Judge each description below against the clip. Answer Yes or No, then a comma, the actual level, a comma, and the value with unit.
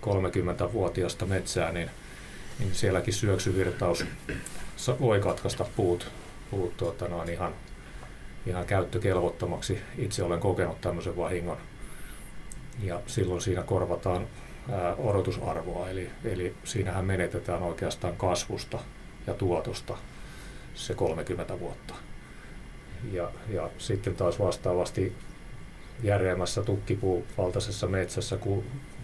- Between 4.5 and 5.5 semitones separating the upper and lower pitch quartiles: No, average, 2.9 semitones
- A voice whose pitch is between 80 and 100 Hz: Yes, very low, 95 Hz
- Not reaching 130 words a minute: Yes, average, 100 wpm